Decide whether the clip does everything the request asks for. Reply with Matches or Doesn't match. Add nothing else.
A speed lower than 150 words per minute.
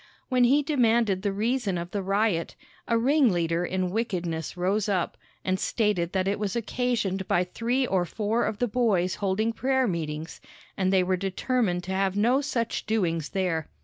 Doesn't match